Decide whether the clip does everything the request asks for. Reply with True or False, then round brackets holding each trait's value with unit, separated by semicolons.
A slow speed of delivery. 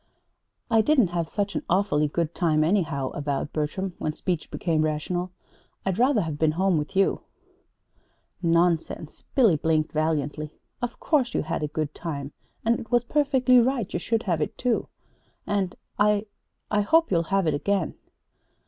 False (165 wpm)